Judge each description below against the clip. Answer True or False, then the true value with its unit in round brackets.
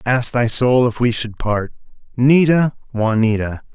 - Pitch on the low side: True (120 Hz)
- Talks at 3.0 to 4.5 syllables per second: True (4.4 syllables/s)